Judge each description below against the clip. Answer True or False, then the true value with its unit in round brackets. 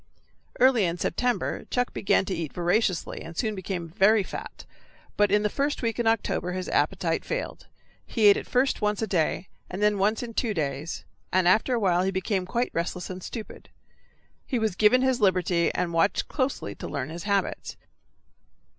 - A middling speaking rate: True (180 wpm)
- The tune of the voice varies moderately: True (4.2 semitones)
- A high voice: True (200 Hz)